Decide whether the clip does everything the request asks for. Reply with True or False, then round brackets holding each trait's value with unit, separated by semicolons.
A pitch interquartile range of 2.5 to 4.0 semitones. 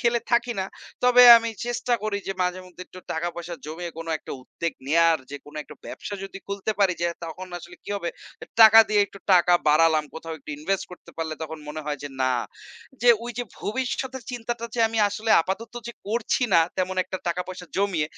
False (5.3 semitones)